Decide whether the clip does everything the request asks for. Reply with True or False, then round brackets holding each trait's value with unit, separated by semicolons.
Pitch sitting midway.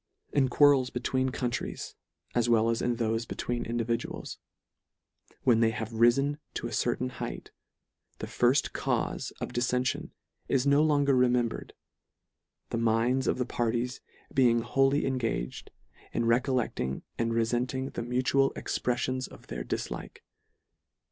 False (120 Hz)